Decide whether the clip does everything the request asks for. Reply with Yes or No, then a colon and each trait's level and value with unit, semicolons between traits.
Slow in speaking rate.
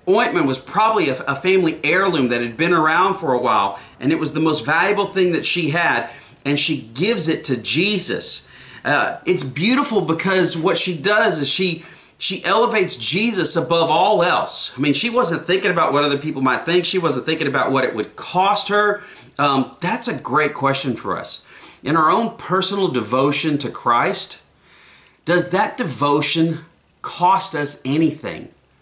No: average, 175 wpm